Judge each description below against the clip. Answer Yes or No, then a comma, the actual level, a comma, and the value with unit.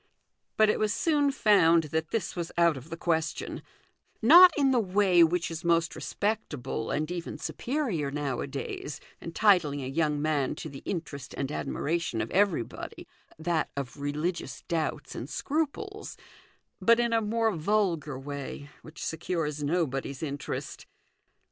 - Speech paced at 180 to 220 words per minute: No, average, 145 wpm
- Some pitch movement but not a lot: No, wide, 6.1 semitones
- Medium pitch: Yes, medium, 165 Hz